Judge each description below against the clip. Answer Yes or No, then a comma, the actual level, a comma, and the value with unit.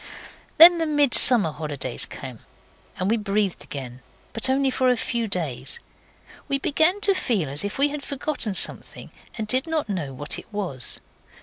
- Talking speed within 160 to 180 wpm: Yes, average, 170 wpm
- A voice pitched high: Yes, high, 220 Hz